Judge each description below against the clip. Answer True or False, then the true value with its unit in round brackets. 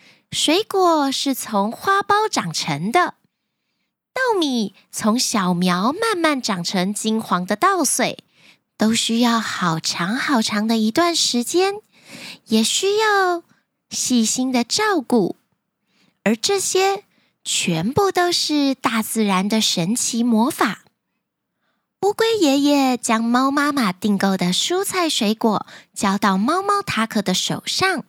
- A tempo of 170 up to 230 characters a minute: True (175 characters per minute)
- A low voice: False (240 Hz)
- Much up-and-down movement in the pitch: True (8.7 semitones)